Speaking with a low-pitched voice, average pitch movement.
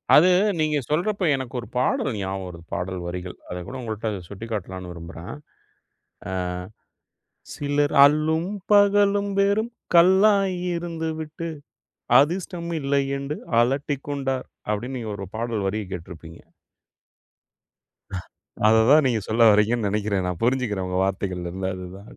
No: low, 120 Hz; wide, 8.3 semitones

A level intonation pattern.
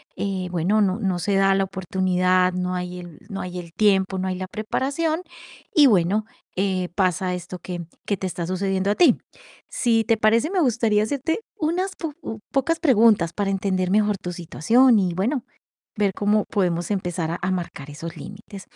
No: average, 3.2 semitones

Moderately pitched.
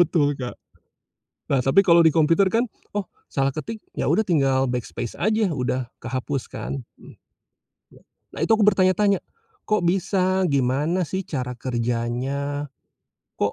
Yes: medium, 150 Hz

